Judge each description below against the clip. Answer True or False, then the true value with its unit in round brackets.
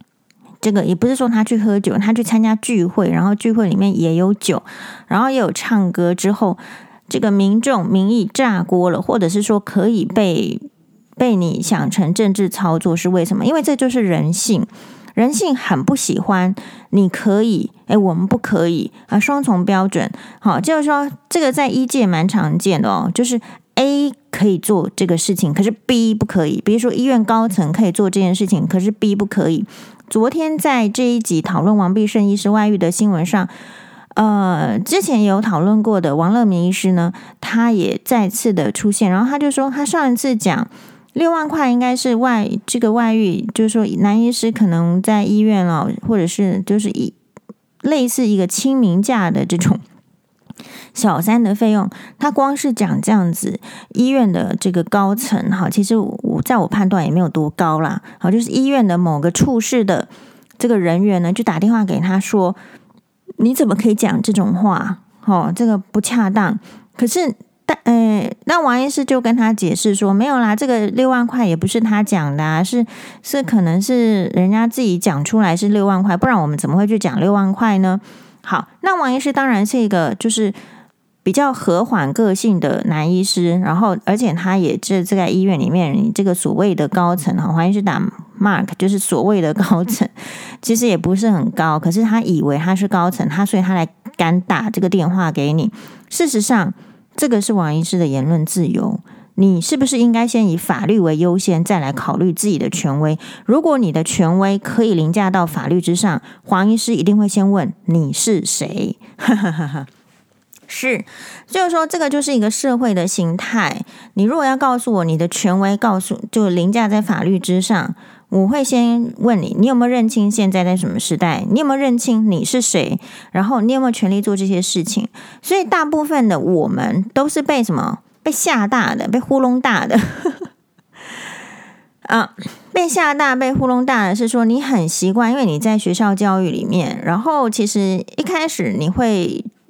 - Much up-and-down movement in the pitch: False (3.9 semitones)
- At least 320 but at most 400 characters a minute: False (275 characters per minute)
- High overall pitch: True (210 Hz)